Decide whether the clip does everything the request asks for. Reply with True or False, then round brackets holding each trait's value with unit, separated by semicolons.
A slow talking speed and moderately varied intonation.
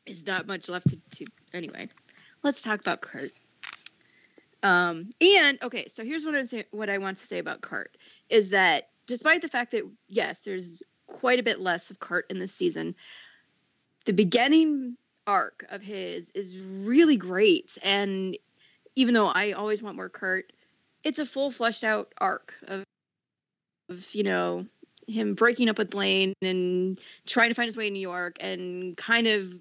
False (175 wpm; 4.7 semitones)